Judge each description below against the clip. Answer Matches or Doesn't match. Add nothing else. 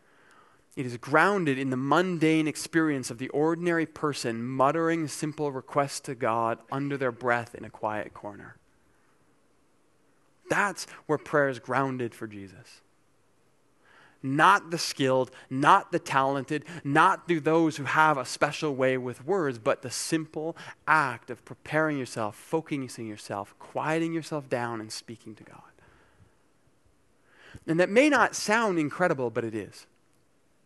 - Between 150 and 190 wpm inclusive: Doesn't match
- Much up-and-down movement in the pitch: Doesn't match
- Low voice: Doesn't match